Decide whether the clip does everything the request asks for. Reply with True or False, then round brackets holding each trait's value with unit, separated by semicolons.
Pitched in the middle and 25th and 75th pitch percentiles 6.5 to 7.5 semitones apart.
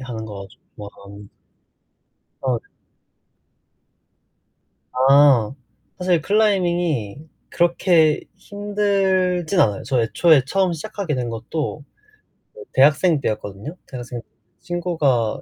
True (150 Hz; 6.8 semitones)